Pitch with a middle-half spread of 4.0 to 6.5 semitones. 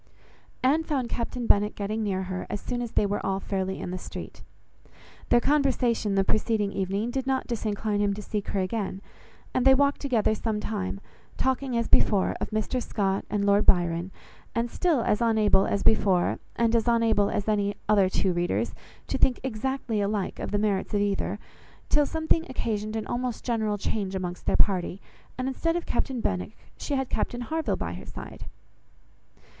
No: average, 3.6 semitones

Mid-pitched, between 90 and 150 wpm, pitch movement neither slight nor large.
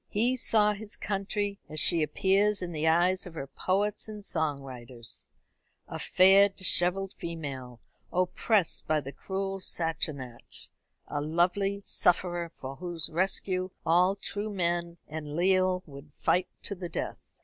Yes: medium, 180 Hz; average, 140 wpm; average, 3.7 semitones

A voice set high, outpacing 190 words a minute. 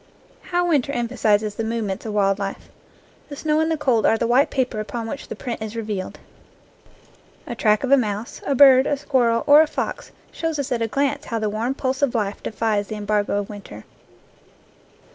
Yes: high, 230 Hz; average, 200 wpm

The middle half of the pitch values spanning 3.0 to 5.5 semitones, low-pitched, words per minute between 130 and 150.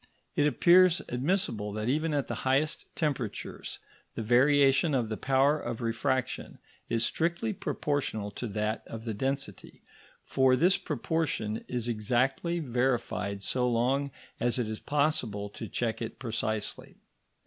Yes: average, 4.5 semitones; low, 125 Hz; slow, 135 wpm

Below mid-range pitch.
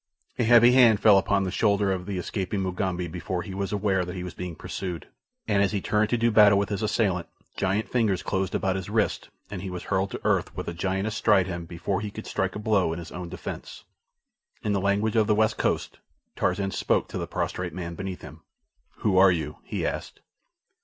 Yes: very low, 95 Hz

